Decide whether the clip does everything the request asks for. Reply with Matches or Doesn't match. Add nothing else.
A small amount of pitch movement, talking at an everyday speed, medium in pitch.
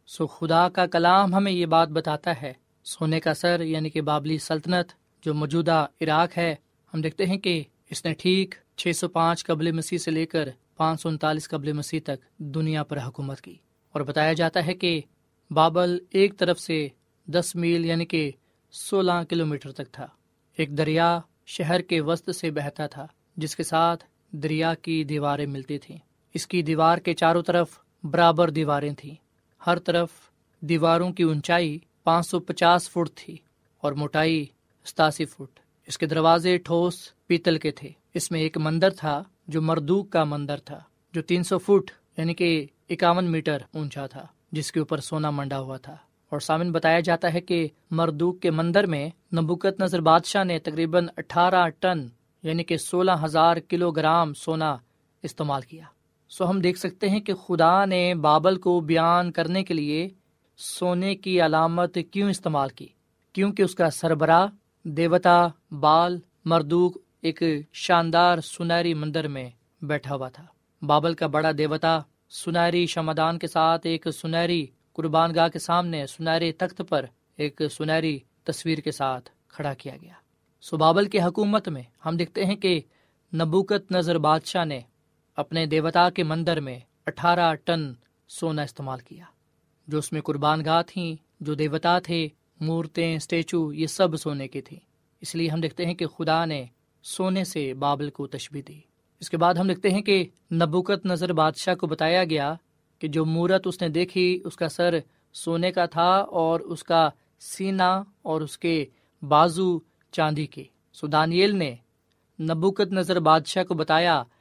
Matches